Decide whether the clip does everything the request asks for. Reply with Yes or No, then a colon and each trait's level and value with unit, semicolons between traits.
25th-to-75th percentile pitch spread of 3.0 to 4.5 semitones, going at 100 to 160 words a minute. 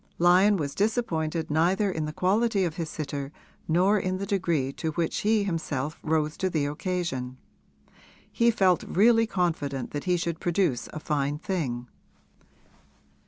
Yes: average, 4.2 semitones; average, 150 wpm